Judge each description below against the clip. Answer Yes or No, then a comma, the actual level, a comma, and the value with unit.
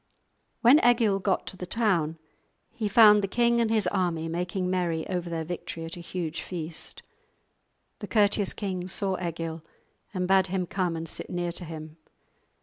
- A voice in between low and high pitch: Yes, medium, 180 Hz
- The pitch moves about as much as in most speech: Yes, average, 3.4 semitones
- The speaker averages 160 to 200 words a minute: Yes, average, 170 wpm